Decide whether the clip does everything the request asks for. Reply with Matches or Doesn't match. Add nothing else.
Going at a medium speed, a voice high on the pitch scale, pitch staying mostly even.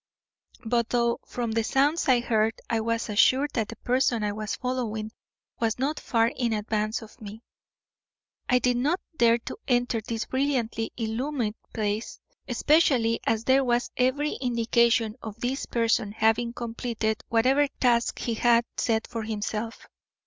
Matches